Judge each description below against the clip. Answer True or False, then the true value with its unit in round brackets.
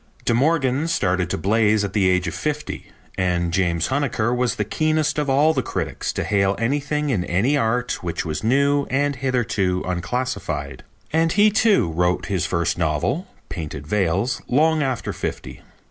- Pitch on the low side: True (115 Hz)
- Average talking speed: True (165 wpm)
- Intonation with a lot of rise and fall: True (7.8 semitones)